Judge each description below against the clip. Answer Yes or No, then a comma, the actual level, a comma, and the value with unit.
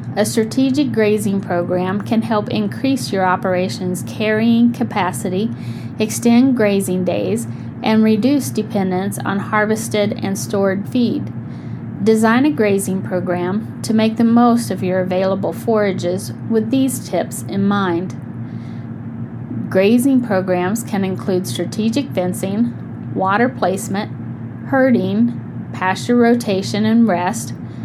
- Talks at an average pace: No, slow, 110 wpm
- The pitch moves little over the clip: No, average, 3.8 semitones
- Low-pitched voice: No, high, 205 Hz